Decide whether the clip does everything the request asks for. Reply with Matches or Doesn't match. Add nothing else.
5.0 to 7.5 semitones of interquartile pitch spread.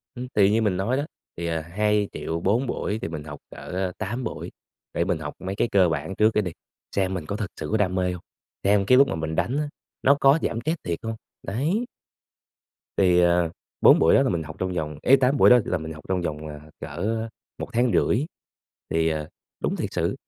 Matches